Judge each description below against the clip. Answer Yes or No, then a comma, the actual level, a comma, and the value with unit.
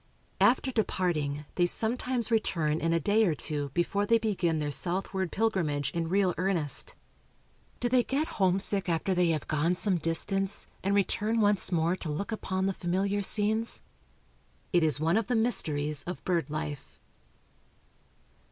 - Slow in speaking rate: No, average, 155 wpm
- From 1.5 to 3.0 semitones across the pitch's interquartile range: No, average, 4.3 semitones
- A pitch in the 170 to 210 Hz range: Yes, medium, 185 Hz